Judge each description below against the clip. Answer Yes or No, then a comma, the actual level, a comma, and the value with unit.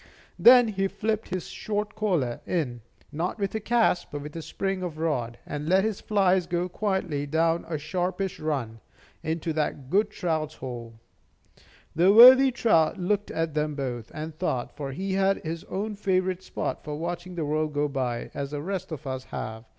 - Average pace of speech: Yes, average, 180 wpm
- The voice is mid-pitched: Yes, medium, 165 Hz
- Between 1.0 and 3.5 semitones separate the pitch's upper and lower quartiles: No, average, 4.8 semitones